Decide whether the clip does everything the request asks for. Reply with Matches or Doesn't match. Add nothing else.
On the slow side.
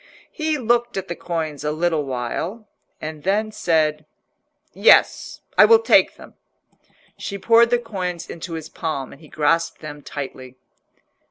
Doesn't match